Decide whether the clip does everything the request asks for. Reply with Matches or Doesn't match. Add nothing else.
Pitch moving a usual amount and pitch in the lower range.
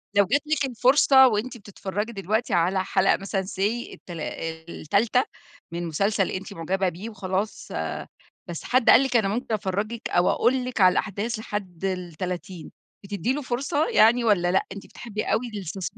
Doesn't match